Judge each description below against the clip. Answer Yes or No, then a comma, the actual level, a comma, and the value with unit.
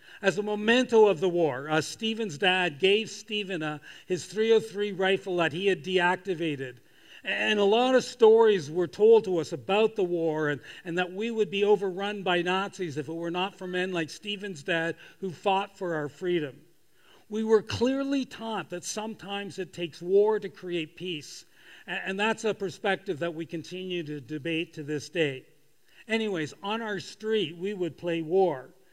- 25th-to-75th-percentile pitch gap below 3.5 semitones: No, average, 3.8 semitones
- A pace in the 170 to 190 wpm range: Yes, average, 180 wpm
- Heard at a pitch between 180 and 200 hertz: Yes, medium, 185 Hz